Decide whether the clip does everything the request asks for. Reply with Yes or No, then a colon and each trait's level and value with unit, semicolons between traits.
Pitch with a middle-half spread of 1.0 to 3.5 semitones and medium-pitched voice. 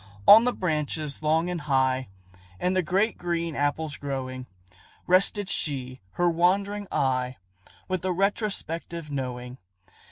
No: wide, 5.5 semitones; medium, 160 Hz